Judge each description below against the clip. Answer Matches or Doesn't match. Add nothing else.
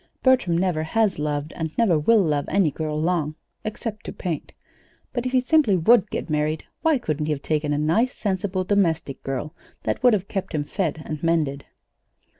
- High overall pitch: Doesn't match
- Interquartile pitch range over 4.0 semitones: Matches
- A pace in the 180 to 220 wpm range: Matches